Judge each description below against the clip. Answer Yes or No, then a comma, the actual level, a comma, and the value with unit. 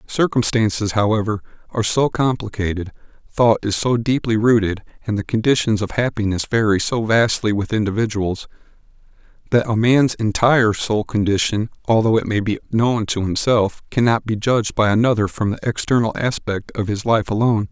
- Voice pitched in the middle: No, low, 110 Hz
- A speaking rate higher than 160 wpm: No, average, 155 wpm